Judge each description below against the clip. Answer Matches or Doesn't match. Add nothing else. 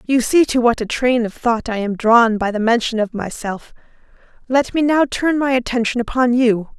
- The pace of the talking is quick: Matches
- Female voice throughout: Matches